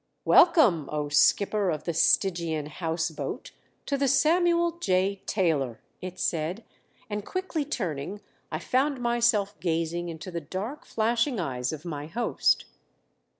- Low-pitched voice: No, medium, 185 Hz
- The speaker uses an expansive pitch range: Yes, wide, 6.9 semitones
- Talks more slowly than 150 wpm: Yes, slow, 135 wpm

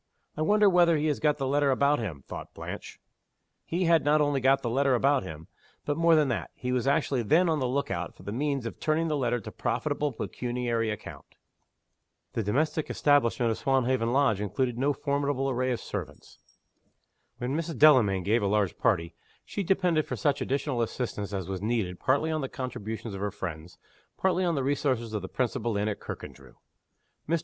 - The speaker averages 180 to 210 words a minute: Yes, average, 195 wpm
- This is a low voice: Yes, low, 130 Hz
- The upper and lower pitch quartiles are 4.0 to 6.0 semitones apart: Yes, average, 4.7 semitones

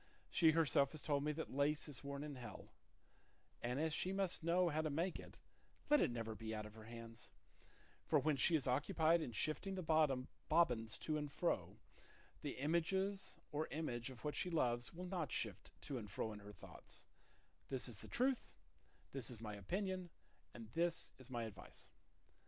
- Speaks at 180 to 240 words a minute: Yes, average, 185 wpm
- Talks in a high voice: No, medium, 145 Hz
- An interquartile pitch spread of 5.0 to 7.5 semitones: Yes, wide, 5.5 semitones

